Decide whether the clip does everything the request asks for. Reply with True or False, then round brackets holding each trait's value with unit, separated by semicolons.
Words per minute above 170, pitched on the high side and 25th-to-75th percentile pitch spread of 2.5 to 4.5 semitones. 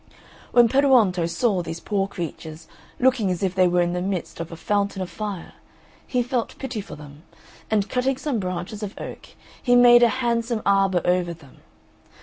False (180 wpm; 200 Hz; 5.3 semitones)